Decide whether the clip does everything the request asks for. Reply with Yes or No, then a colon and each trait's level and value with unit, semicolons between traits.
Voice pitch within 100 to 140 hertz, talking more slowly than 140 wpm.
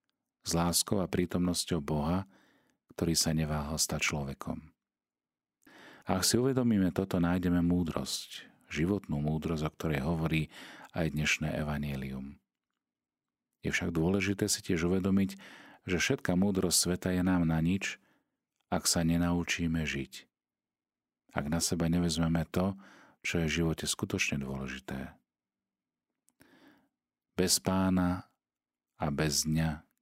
No: very low, 85 Hz; average, 115 wpm